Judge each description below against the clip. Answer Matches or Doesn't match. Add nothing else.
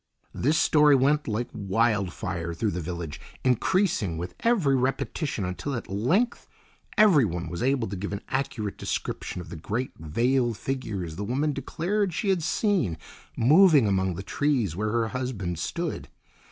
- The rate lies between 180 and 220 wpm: Doesn't match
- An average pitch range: Doesn't match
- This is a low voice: Matches